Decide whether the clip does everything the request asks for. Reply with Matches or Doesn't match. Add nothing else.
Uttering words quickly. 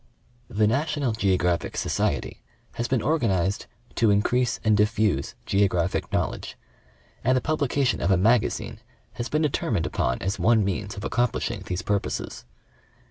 Doesn't match